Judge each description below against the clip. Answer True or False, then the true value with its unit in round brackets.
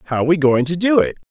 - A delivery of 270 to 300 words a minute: True (275 wpm)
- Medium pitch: True (160 Hz)